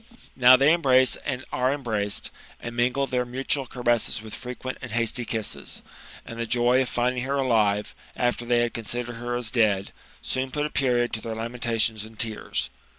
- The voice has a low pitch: Yes, low, 120 Hz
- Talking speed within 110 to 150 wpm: No, average, 175 wpm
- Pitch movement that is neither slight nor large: No, narrow, 2.1 semitones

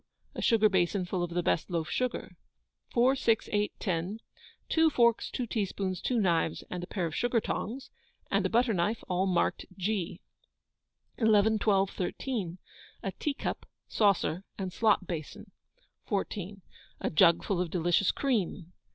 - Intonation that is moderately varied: Yes, average, 4.1 semitones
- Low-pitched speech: No, high, 195 Hz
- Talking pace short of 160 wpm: Yes, average, 150 wpm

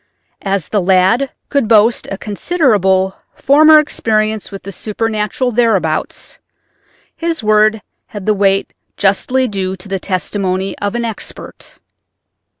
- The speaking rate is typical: No, slow, 125 wpm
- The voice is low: No, high, 210 Hz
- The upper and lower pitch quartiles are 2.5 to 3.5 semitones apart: Yes, average, 3.2 semitones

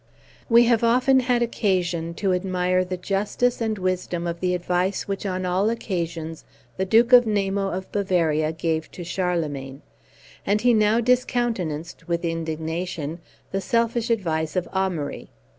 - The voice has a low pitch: No, medium, 185 Hz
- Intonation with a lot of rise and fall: No, average, 4.3 semitones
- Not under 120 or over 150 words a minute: Yes, average, 140 wpm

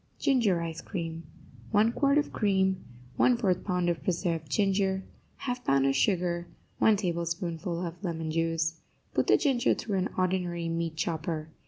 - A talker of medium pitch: Yes, medium, 175 Hz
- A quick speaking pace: No, average, 150 wpm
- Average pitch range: Yes, average, 3.0 semitones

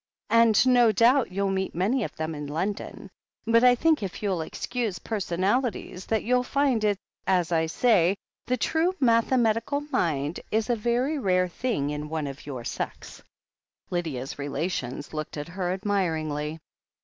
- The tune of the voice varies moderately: No, wide, 6.6 semitones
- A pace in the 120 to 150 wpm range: No, average, 160 wpm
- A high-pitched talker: Yes, high, 195 Hz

